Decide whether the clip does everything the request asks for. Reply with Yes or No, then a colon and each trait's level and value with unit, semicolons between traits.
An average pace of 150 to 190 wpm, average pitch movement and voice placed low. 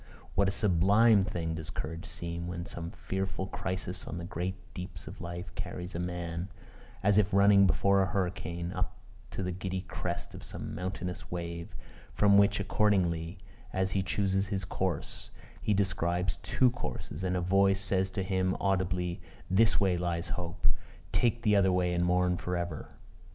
No: average, 170 wpm; narrow, 1.9 semitones; very low, 95 Hz